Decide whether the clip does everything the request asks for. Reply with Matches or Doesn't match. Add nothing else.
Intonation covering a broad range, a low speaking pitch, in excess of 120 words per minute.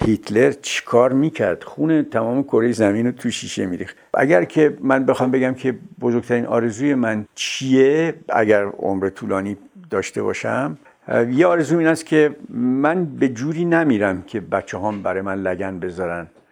Matches